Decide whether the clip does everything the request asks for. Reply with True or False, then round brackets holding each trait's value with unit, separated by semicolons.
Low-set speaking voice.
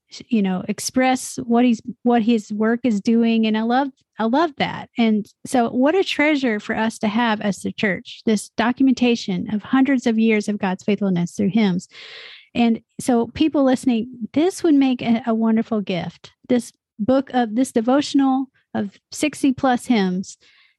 False (235 Hz)